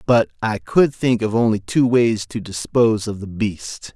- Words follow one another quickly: No, average, 195 wpm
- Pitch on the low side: Yes, low, 110 Hz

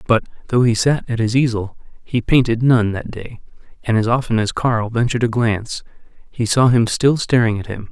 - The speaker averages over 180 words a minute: Yes, fast, 205 wpm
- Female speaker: No, male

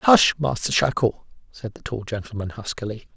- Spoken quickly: No, average, 150 wpm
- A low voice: Yes, low, 115 Hz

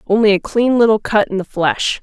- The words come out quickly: Yes, fast, 235 wpm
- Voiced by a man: No, female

